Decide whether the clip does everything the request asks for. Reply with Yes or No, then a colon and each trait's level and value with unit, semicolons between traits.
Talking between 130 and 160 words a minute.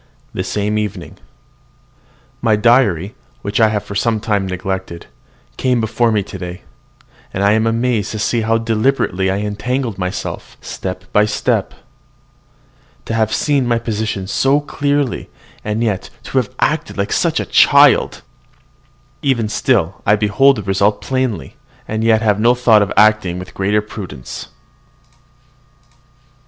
Yes: average, 145 wpm